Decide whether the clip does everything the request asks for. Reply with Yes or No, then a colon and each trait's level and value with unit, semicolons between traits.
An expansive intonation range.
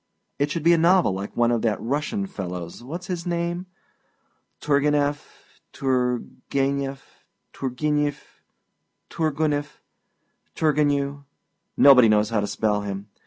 No: average, 4.4 semitones